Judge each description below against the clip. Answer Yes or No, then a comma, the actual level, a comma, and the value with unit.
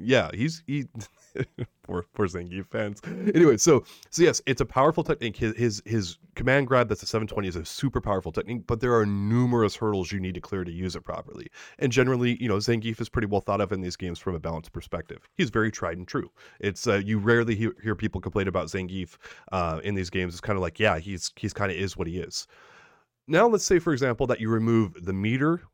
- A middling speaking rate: No, fast, 230 wpm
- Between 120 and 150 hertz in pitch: No, low, 105 Hz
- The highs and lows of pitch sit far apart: No, average, 4.2 semitones